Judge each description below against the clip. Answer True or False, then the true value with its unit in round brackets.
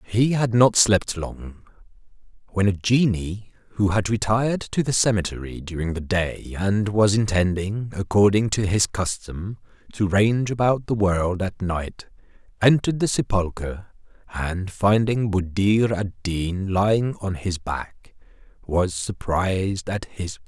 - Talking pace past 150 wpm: False (140 wpm)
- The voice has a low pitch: True (100 Hz)